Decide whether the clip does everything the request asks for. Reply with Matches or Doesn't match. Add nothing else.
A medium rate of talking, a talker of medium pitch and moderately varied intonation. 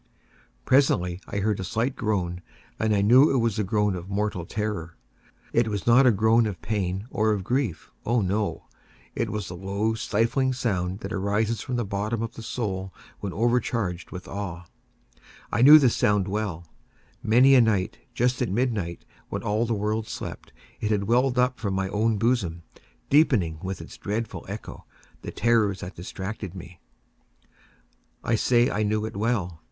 Doesn't match